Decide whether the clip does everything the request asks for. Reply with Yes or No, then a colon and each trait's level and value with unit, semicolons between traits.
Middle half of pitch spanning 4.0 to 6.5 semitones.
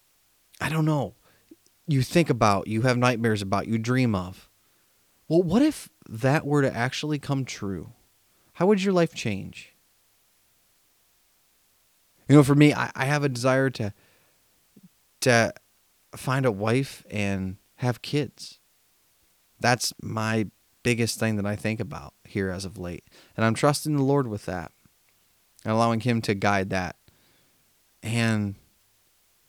Yes: average, 5.2 semitones